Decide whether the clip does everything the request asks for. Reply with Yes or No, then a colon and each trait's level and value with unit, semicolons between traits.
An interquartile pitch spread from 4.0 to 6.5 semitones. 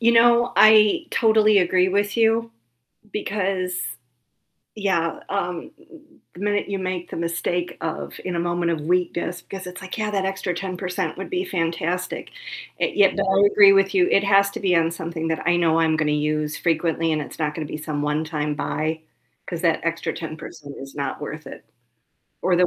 No: average, 3.3 semitones